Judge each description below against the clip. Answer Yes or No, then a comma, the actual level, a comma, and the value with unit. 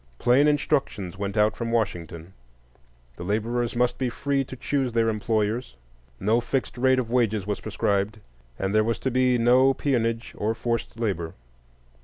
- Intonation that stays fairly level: No, average, 3.2 semitones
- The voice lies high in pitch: No, low, 115 Hz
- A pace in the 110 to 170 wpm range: Yes, average, 160 wpm